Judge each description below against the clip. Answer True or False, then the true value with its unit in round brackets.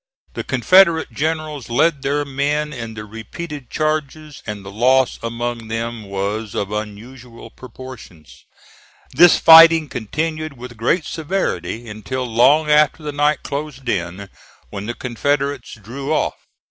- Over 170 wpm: False (135 wpm)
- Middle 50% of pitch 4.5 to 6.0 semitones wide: True (5.0 semitones)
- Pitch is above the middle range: False (130 Hz)